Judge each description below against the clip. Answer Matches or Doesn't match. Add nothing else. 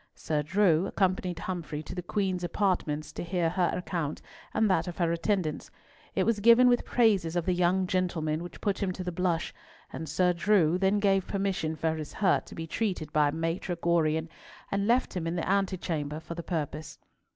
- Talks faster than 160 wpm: Matches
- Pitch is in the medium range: Matches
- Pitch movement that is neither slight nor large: Matches